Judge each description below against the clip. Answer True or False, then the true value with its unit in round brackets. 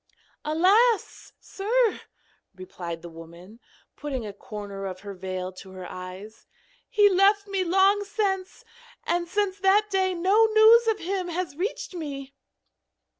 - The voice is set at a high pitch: True (355 Hz)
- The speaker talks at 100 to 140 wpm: True (135 wpm)